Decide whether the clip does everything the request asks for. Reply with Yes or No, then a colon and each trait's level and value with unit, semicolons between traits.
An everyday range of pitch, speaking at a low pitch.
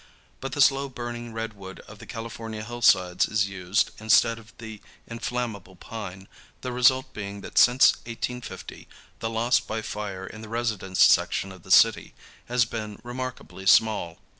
Yes: average, 3.1 semitones; low, 110 Hz